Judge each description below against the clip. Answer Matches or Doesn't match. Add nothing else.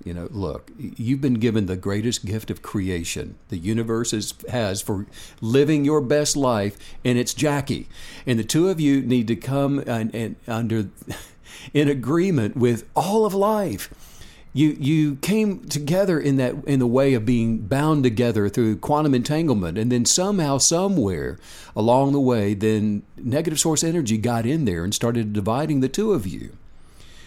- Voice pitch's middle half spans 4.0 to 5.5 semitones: Matches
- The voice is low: Matches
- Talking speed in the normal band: Matches